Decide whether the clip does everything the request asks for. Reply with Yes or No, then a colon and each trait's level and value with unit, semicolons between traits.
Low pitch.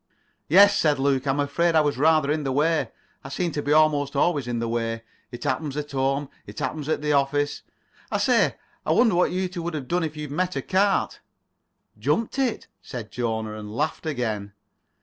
No: medium, 145 Hz